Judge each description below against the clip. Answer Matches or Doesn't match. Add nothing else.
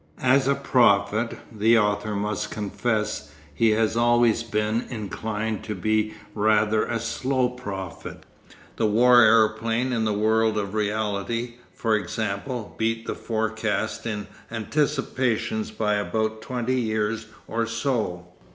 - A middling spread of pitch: Doesn't match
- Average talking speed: Doesn't match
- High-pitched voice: Doesn't match